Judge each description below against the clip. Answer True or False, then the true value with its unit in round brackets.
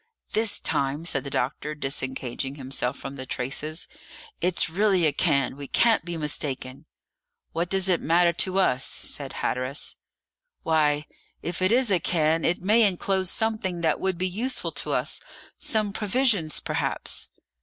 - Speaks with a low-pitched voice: False (165 Hz)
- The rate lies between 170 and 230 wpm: False (155 wpm)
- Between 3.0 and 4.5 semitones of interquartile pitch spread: False (5.2 semitones)